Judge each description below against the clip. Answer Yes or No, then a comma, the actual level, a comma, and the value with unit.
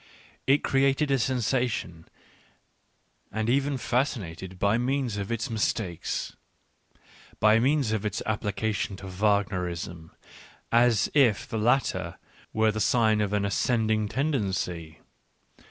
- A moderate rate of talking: No, slow, 120 wpm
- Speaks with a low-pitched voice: Yes, low, 110 Hz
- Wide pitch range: No, average, 4.1 semitones